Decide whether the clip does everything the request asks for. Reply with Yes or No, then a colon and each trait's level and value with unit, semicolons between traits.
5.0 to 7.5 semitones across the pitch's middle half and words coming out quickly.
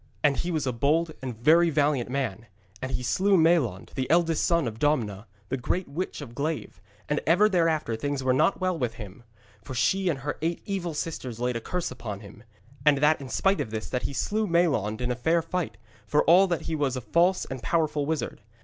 Yes: average, 5.3 semitones; fast, 215 wpm